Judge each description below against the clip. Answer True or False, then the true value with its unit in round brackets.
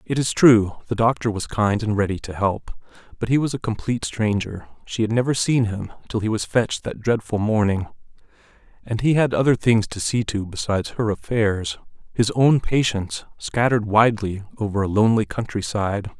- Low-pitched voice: True (110 Hz)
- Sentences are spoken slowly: False (180 wpm)